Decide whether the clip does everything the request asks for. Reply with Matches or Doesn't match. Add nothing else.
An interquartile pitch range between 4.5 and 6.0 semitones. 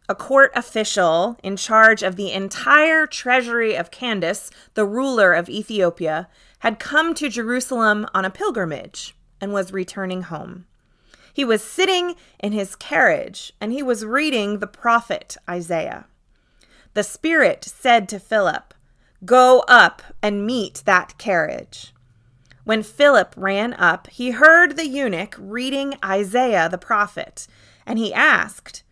Matches